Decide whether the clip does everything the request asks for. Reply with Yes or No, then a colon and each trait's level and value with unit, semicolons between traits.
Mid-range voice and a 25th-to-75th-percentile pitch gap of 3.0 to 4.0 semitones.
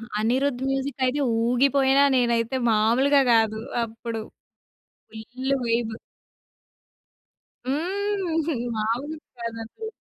No: very high, 255 Hz; average, 3.6 semitones